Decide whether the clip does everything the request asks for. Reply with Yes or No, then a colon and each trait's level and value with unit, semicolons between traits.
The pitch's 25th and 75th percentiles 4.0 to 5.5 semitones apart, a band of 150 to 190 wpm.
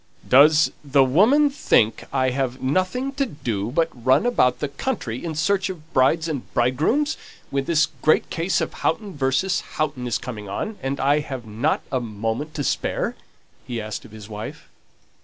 Yes: average, 5.0 semitones; average, 170 wpm